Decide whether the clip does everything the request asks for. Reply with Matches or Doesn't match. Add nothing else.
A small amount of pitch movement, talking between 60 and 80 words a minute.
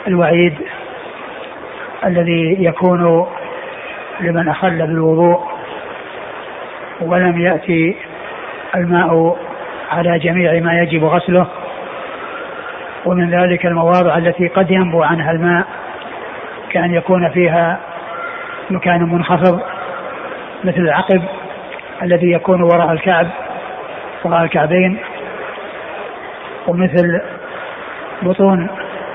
Matches